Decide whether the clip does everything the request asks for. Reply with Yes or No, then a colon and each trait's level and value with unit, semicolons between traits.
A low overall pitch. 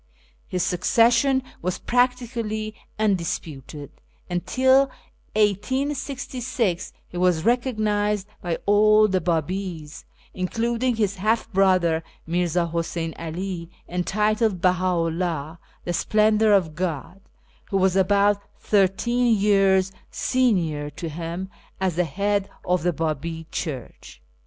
No: high, 190 Hz